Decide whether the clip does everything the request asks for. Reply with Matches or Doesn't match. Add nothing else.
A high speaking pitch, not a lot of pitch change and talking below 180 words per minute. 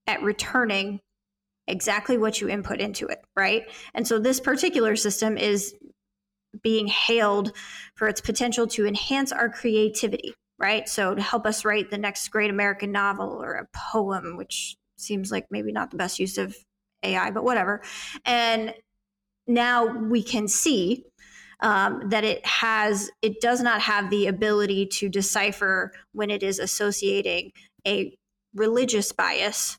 Matches